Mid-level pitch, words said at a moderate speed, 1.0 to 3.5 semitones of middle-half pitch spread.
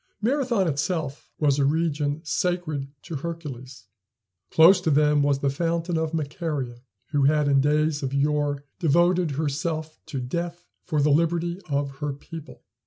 Yes: medium, 150 Hz; average, 150 wpm; average, 2.9 semitones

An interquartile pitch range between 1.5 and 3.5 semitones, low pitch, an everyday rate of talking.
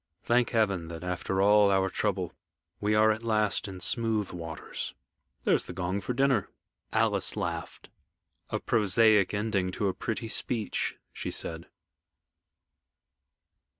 No: average, 3.0 semitones; low, 105 Hz; slow, 130 wpm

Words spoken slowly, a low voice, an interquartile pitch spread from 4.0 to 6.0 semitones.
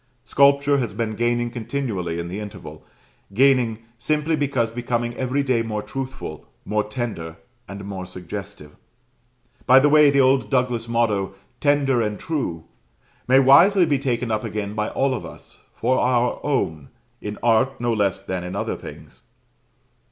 No: average, 155 wpm; low, 120 Hz; average, 4.5 semitones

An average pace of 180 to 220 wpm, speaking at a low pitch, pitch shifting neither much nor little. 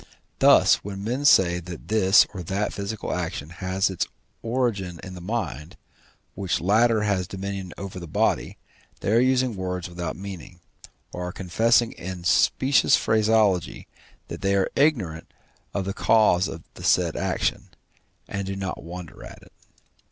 No: average, 155 wpm; very low, 95 Hz; average, 3.4 semitones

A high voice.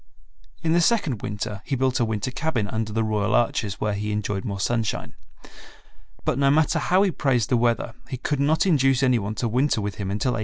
No: low, 120 Hz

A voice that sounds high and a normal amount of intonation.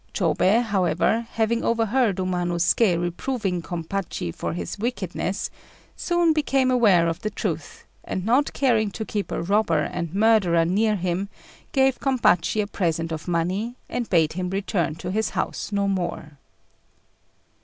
Yes: high, 195 Hz; average, 4.6 semitones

